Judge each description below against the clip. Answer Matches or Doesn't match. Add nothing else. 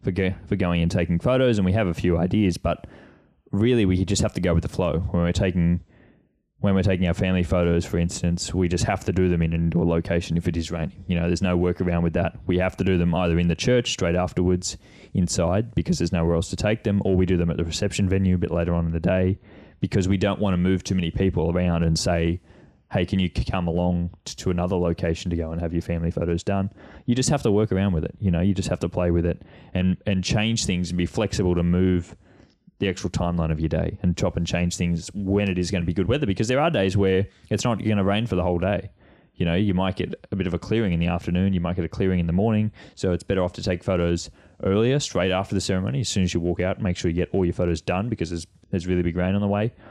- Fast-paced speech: Matches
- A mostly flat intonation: Matches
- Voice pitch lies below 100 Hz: Matches